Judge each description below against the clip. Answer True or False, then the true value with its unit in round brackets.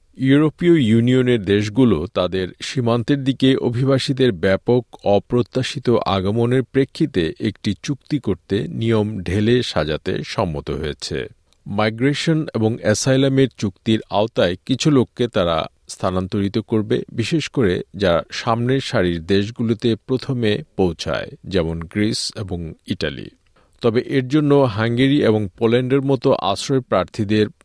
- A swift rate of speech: False (110 wpm)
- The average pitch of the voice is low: True (115 Hz)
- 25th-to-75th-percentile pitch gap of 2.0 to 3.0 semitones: False (4.4 semitones)